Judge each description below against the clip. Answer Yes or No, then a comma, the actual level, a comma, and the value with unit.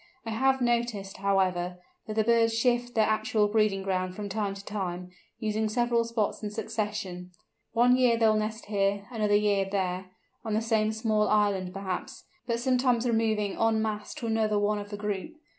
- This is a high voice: Yes, high, 215 Hz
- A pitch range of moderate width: No, narrow, 2.3 semitones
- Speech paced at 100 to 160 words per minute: No, average, 180 wpm